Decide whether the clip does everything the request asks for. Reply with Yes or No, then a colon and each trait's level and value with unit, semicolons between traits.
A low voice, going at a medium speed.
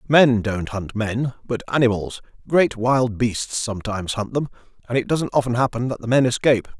Yes: low, 120 Hz; average, 185 wpm